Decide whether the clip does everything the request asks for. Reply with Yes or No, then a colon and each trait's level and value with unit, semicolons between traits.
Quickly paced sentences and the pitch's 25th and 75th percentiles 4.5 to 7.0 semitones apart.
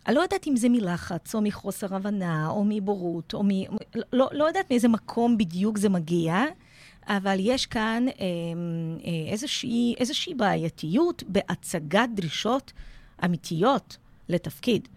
No: average, 125 wpm; wide, 5.5 semitones